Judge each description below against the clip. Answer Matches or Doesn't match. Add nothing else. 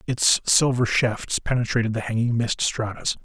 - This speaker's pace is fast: Doesn't match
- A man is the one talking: Matches